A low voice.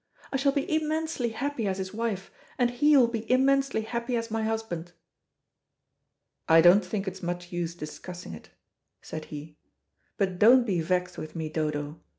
No: high, 205 Hz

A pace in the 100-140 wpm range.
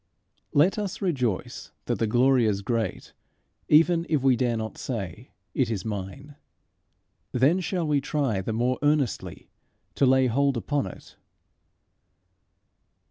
Yes: slow, 135 wpm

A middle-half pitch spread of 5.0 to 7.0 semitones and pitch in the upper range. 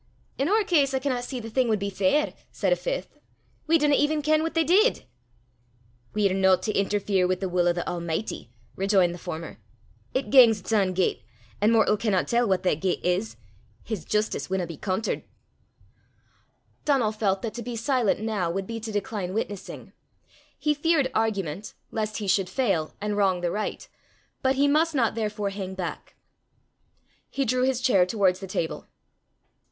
Yes: wide, 5.4 semitones; high, 210 Hz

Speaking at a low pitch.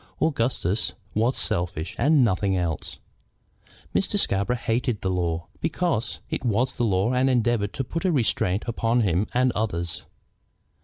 Yes: low, 115 Hz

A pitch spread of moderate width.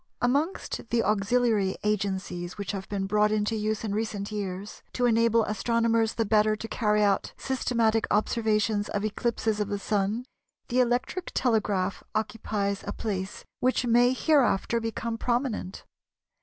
No: narrow, 2.3 semitones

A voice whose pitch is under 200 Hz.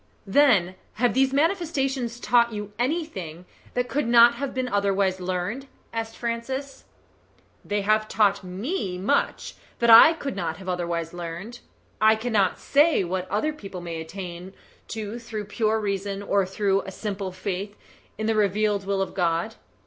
No: high, 210 Hz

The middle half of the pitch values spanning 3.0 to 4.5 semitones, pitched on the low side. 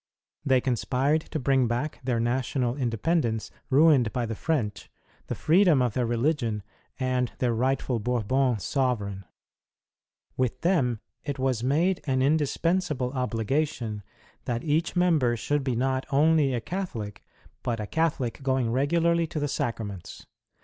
Yes: average, 4.0 semitones; low, 130 Hz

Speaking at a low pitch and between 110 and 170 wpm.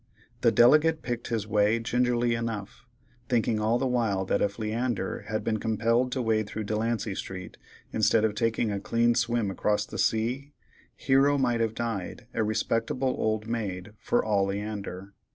Yes: low, 115 Hz; average, 165 wpm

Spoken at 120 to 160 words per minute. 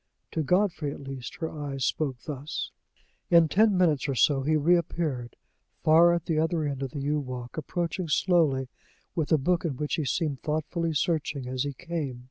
No: average, 185 wpm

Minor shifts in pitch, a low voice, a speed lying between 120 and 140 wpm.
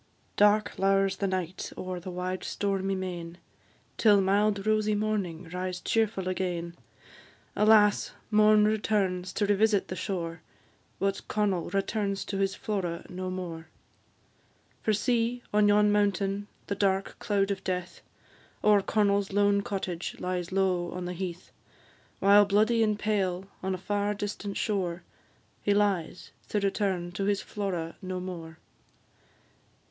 No: narrow, 2.1 semitones; high, 195 Hz; slow, 135 wpm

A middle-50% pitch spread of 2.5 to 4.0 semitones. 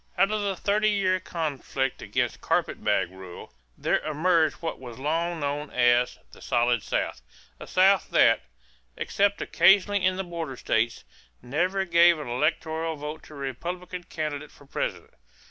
No: average, 5.1 semitones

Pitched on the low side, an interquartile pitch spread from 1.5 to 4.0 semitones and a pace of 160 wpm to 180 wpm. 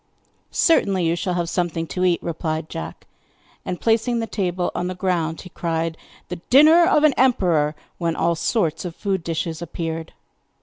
No: medium, 175 Hz; average, 3.1 semitones; average, 170 wpm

